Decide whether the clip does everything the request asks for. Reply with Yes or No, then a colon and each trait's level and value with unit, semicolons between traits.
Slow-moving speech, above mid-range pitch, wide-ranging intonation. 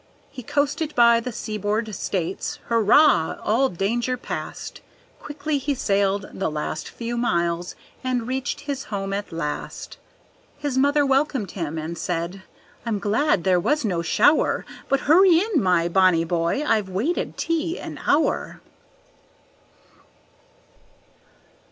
Yes: slow, 125 wpm; high, 225 Hz; wide, 7.3 semitones